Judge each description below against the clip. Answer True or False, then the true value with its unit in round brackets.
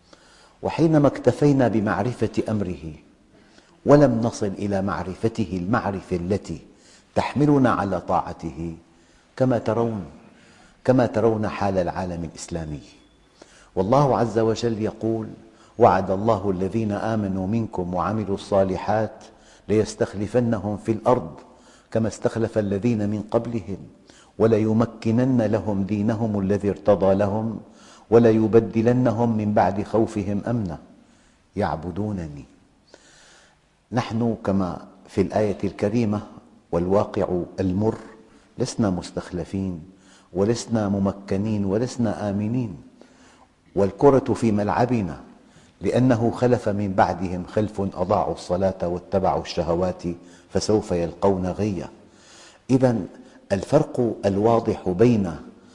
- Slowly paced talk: True (90 wpm)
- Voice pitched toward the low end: True (105 Hz)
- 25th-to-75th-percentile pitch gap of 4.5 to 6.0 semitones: False (3.0 semitones)